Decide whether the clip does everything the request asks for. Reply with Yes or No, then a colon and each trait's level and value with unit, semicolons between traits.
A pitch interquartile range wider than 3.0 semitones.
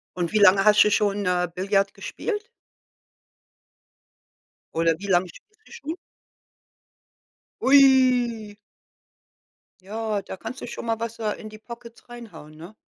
Yes: average, 3.5 semitones